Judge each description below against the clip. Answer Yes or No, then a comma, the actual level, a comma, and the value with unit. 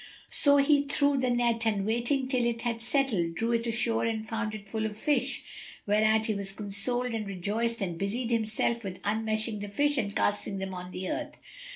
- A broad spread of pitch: No, average, 2.9 semitones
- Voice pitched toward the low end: No, high, 225 Hz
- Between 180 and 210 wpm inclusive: Yes, average, 200 wpm